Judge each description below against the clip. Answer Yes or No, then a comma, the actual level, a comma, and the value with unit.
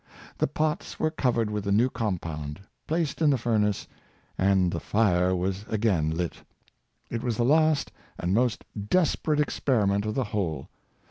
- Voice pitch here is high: No, low, 105 Hz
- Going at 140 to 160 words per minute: Yes, average, 150 wpm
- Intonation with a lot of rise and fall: Yes, wide, 5.9 semitones